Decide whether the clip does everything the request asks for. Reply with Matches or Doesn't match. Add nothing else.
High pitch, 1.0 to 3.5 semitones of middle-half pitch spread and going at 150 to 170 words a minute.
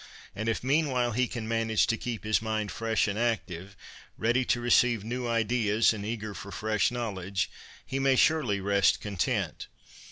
Doesn't match